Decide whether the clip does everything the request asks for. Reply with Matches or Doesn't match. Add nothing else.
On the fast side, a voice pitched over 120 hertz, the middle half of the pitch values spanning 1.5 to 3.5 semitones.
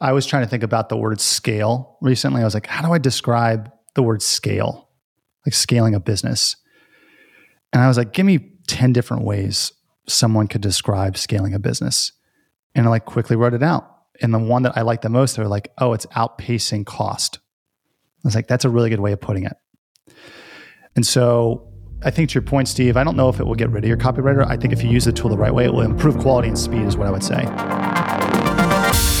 Doesn't match